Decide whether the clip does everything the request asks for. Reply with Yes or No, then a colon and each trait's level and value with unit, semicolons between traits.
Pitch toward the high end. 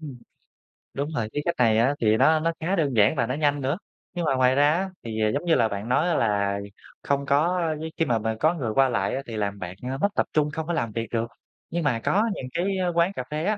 No: medium, 140 Hz